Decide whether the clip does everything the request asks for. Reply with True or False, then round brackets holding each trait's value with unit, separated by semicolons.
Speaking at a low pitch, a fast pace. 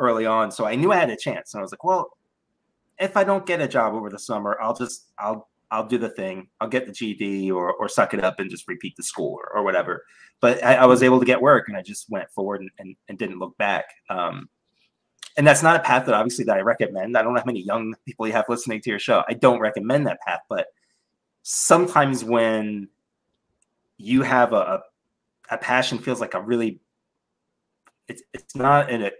True (115 Hz; 230 wpm)